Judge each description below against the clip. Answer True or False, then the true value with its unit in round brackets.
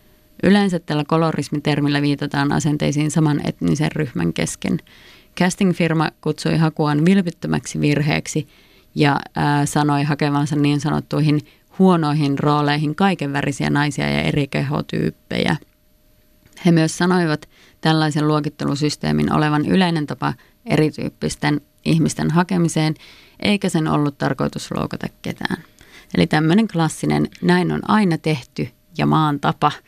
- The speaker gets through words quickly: False (110 wpm)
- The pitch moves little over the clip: True (2.2 semitones)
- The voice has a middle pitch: True (150 Hz)